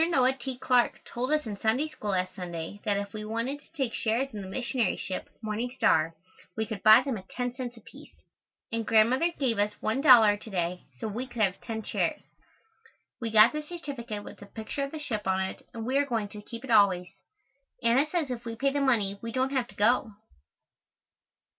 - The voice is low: No, high, 230 Hz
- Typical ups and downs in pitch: Yes, average, 4.0 semitones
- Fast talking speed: Yes, fast, 210 wpm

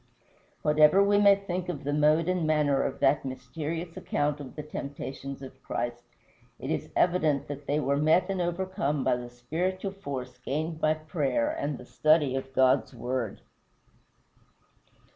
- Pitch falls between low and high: Yes, medium, 150 Hz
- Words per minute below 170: Yes, average, 160 wpm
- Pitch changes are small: No, average, 3.9 semitones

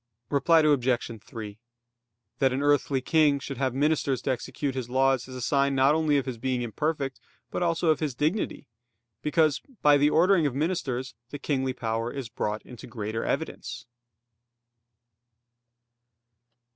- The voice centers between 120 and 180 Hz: Yes, low, 135 Hz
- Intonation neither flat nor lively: Yes, average, 3.1 semitones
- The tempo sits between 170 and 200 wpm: No, average, 150 wpm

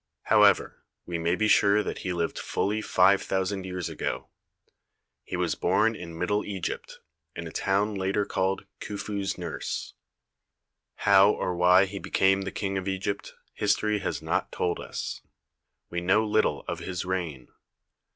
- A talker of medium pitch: No, very low, 95 Hz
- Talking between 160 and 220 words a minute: No, average, 150 wpm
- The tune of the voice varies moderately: No, narrow, 2.1 semitones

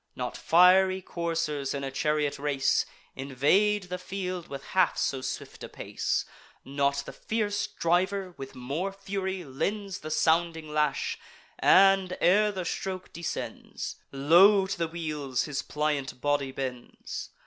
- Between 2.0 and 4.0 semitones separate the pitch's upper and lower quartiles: No, average, 5.2 semitones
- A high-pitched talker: No, medium, 165 Hz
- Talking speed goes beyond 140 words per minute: No, slow, 135 wpm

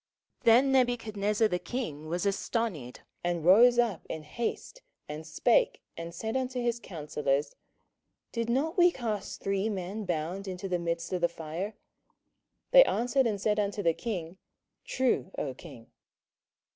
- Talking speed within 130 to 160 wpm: Yes, average, 150 wpm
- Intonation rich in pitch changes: Yes, wide, 5.9 semitones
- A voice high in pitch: Yes, high, 200 Hz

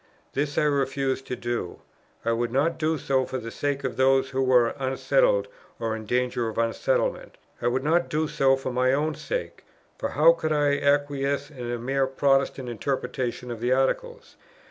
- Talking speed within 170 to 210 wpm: Yes, average, 185 wpm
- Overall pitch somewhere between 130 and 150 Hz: Yes, low, 135 Hz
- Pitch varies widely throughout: No, average, 2.9 semitones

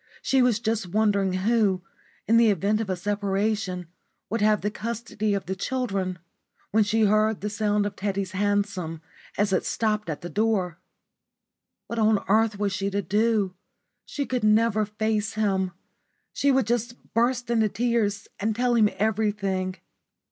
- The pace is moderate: Yes, average, 160 wpm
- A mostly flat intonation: Yes, narrow, 2.1 semitones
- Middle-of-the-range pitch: No, high, 210 Hz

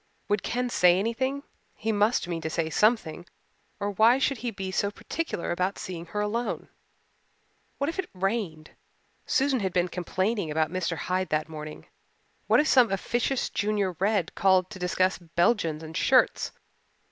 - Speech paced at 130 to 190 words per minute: Yes, average, 160 wpm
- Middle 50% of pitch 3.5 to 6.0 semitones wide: Yes, average, 4.7 semitones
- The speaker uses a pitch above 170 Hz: Yes, high, 190 Hz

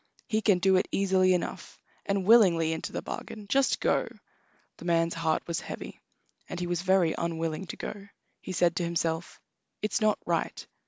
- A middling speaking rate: Yes, average, 175 wpm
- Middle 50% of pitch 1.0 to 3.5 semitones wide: Yes, average, 2.9 semitones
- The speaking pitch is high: No, medium, 180 Hz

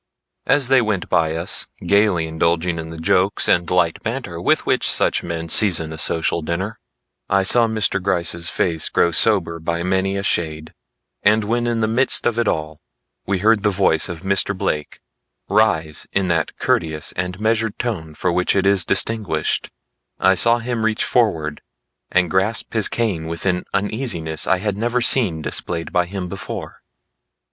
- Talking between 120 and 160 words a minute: No, average, 170 wpm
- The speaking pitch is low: Yes, very low, 95 Hz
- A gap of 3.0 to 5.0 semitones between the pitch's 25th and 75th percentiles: Yes, average, 4.6 semitones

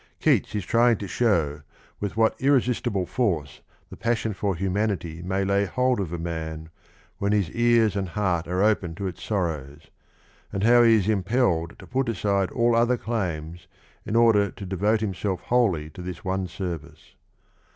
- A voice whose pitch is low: Yes, low, 100 Hz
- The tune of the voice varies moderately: Yes, average, 4.5 semitones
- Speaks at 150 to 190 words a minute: Yes, average, 170 wpm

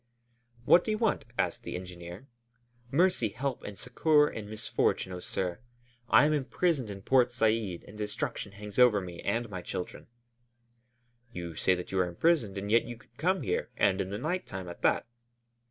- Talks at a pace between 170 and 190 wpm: Yes, average, 185 wpm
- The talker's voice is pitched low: Yes, low, 105 Hz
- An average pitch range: No, wide, 6.4 semitones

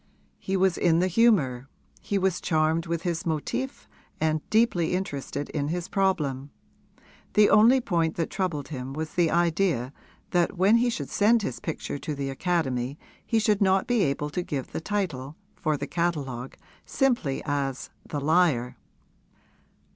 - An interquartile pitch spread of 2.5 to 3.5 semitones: No, average, 5.1 semitones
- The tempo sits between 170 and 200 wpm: No, average, 155 wpm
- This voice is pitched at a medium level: Yes, medium, 165 Hz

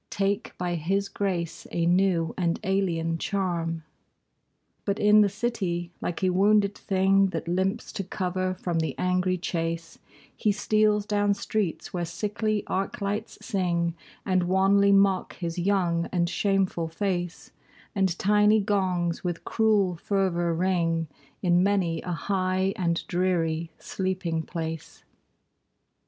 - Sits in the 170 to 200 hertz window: Yes, medium, 185 Hz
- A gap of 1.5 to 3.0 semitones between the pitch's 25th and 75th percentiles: Yes, average, 2.7 semitones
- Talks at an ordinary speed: No, slow, 130 wpm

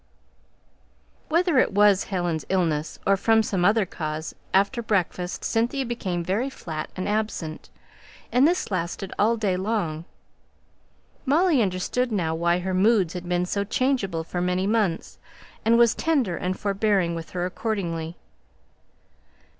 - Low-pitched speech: No, high, 195 Hz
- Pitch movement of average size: Yes, average, 4.3 semitones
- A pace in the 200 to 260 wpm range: No, average, 140 wpm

